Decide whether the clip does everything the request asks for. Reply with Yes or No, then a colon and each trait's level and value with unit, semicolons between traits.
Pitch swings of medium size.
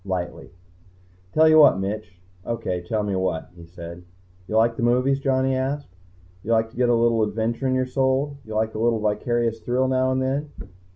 Yes: average, 3.7 semitones